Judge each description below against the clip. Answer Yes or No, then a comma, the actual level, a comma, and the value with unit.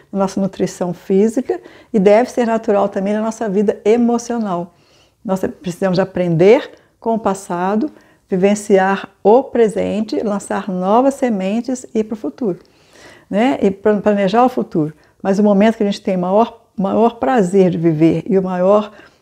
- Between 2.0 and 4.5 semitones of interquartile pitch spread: Yes, average, 2.9 semitones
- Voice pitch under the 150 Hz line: No, high, 205 Hz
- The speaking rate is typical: Yes, average, 155 wpm